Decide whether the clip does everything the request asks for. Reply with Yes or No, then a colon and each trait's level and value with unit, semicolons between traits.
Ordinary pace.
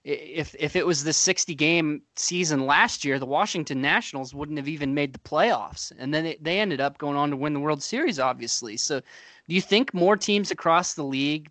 No: fast, 220 wpm